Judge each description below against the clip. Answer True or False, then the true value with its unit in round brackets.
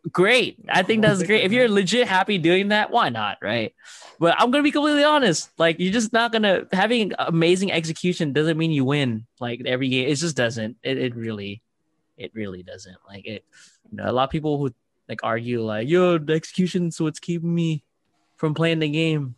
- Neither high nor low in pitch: True (165 Hz)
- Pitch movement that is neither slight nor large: False (6.7 semitones)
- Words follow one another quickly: True (215 wpm)